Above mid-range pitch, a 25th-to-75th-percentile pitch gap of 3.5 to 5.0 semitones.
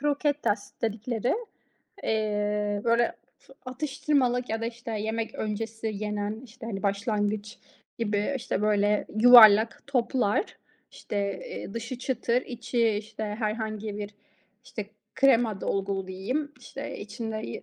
No: high, 220 Hz; average, 2.7 semitones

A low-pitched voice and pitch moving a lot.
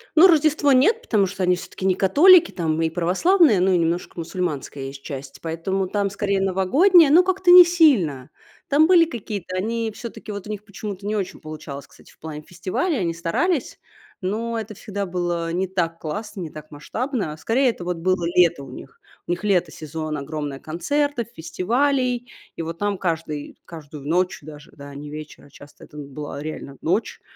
No: medium, 185 Hz; wide, 6.6 semitones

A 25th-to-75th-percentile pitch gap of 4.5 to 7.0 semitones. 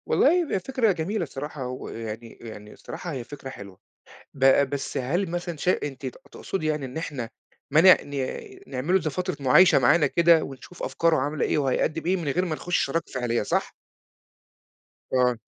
Yes: average, 5.0 semitones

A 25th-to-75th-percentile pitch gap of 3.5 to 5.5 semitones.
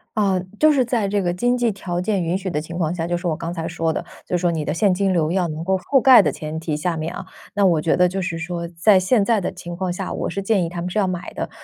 No: average, 2.9 semitones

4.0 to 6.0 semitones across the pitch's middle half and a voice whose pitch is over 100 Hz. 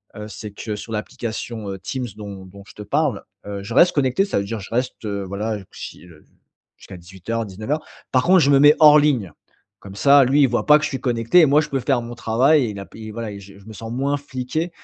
Yes: wide, 5.5 semitones; low, 115 Hz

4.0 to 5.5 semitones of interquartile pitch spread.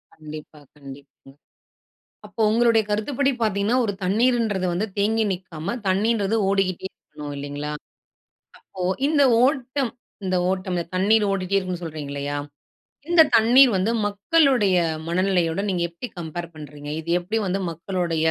Yes: average, 5.2 semitones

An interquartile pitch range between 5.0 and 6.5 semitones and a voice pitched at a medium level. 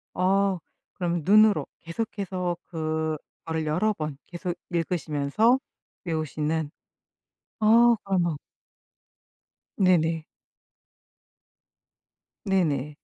No: average, 3.7 semitones; medium, 175 Hz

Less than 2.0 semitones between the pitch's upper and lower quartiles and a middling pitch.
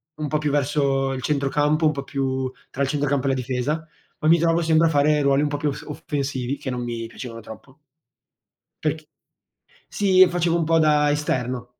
No: narrow, 2.5 semitones; medium, 145 Hz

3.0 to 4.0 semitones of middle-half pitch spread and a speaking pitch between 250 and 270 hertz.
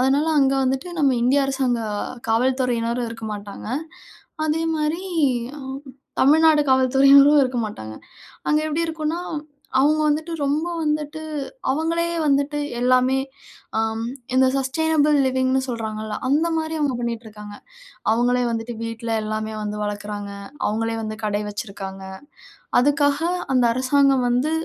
No: average, 4.6 semitones; very high, 260 Hz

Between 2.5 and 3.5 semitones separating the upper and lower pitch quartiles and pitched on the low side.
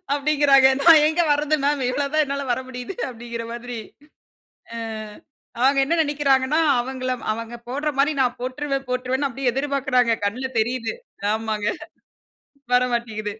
No: average, 2.9 semitones; very high, 260 Hz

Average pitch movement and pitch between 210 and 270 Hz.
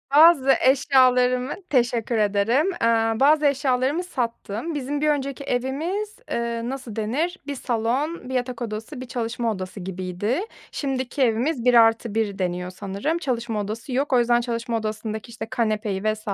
Yes: average, 3.7 semitones; high, 240 Hz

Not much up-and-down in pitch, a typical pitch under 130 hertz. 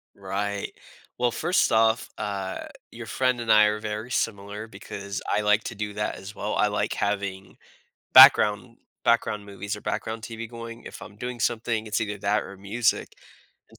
Yes: narrow, 2.1 semitones; low, 105 Hz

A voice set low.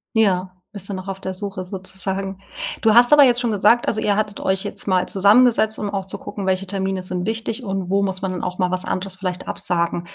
No: high, 195 Hz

